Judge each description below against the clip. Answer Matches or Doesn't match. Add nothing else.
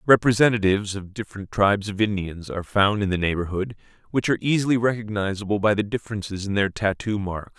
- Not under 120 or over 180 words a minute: Matches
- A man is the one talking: Matches